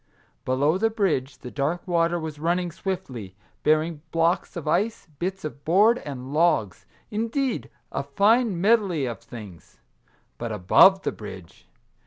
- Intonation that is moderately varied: No, wide, 6.2 semitones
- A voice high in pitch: No, medium, 165 Hz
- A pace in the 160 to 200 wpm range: No, average, 145 wpm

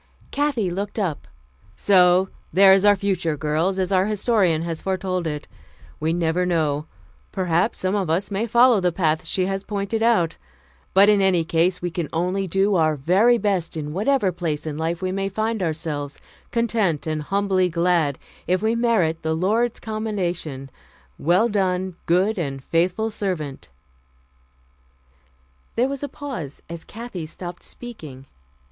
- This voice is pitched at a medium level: Yes, medium, 180 Hz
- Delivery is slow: No, average, 155 wpm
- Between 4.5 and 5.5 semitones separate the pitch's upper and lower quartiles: No, average, 4.1 semitones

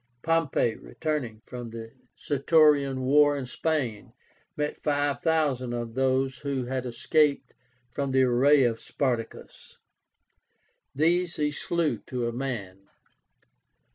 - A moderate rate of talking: No, slow, 115 wpm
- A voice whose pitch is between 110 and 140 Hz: Yes, low, 135 Hz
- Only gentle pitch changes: No, average, 3.5 semitones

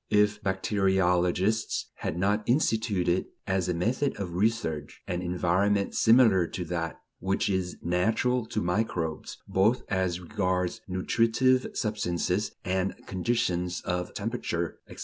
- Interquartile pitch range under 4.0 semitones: Yes, average, 3.5 semitones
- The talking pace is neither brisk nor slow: No, slow, 120 wpm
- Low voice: Yes, very low, 95 Hz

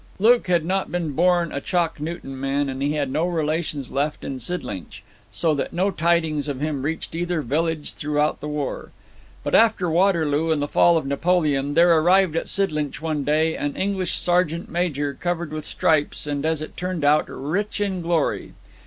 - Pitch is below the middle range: No, medium, 160 Hz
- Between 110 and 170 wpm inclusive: No, average, 185 wpm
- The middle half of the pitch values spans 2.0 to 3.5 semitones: Yes, average, 3.1 semitones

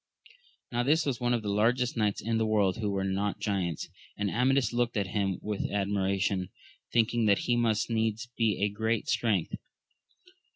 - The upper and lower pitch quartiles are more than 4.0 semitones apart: No, average, 2.9 semitones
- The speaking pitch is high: No, low, 105 Hz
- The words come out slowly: No, average, 175 wpm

